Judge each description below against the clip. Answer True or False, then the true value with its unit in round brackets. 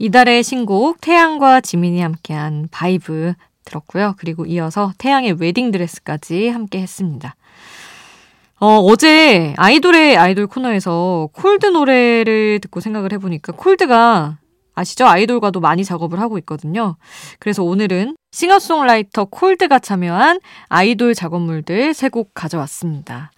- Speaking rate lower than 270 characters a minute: False (325 characters per minute)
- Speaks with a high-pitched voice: True (200 Hz)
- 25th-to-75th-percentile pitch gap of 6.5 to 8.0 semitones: False (6.1 semitones)